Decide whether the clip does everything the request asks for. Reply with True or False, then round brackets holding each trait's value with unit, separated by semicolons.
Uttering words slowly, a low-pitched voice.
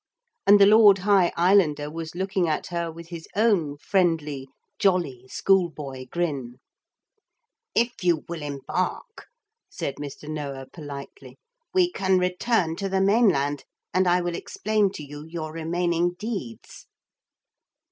False (130 wpm; 170 Hz)